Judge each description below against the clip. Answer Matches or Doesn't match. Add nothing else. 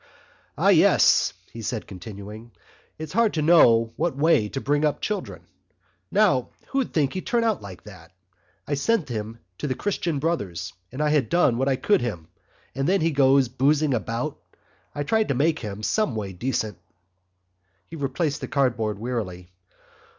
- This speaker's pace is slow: Doesn't match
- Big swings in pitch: Matches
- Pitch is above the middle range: Doesn't match